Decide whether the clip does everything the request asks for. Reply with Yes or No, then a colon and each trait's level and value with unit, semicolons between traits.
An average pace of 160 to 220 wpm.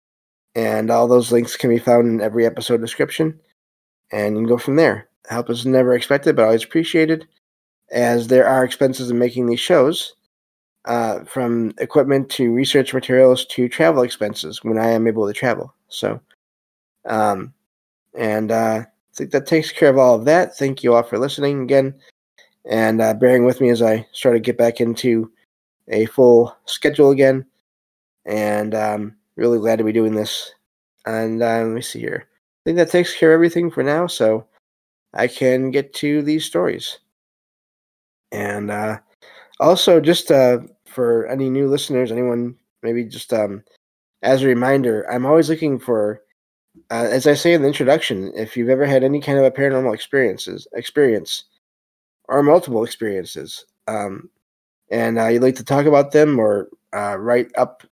Yes: average, 170 wpm